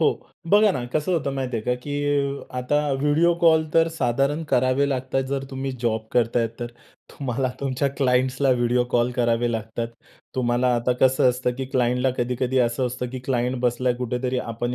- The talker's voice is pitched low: Yes, low, 125 Hz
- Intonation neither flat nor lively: No, narrow, 2.1 semitones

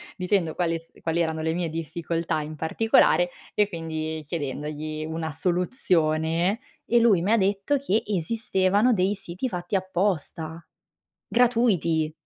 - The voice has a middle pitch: Yes, medium, 170 Hz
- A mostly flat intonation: No, average, 3.8 semitones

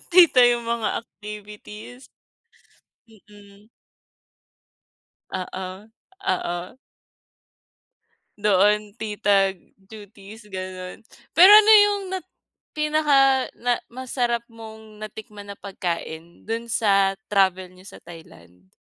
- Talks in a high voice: Yes, high, 210 Hz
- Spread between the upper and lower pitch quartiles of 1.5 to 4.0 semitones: Yes, average, 3.7 semitones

